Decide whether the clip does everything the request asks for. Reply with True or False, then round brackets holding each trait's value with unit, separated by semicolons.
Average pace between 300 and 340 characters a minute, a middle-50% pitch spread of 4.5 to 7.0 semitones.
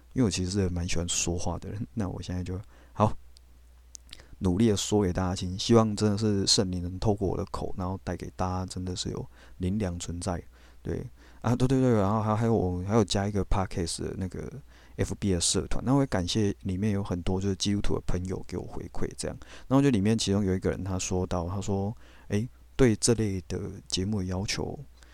False (320 characters per minute; 3.0 semitones)